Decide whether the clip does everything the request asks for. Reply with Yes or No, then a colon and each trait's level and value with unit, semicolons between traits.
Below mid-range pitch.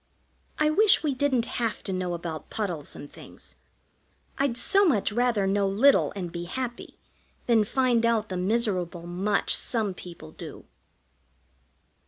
No: high, 210 Hz